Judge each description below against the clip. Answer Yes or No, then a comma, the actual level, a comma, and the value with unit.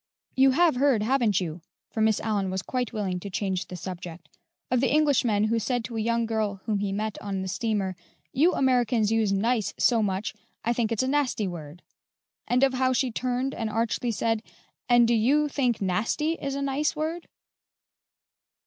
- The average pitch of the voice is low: No, high, 230 Hz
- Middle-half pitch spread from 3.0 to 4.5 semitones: Yes, average, 4.2 semitones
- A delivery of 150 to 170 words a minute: No, average, 190 wpm